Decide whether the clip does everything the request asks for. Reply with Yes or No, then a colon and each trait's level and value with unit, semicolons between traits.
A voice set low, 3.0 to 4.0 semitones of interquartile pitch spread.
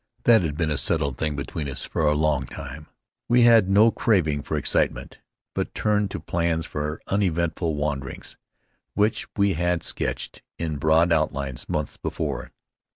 No: very low, 80 Hz; average, 4.5 semitones